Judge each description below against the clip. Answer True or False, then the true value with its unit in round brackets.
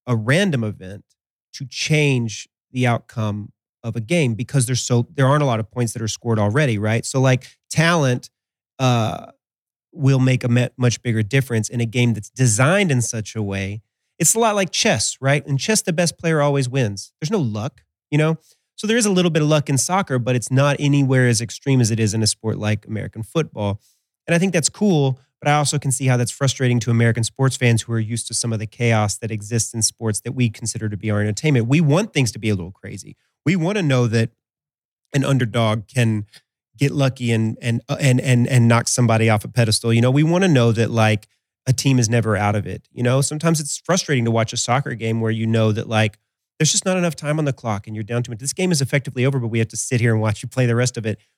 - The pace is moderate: False (250 wpm)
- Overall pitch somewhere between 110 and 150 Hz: True (120 Hz)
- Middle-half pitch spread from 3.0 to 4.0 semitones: True (3.7 semitones)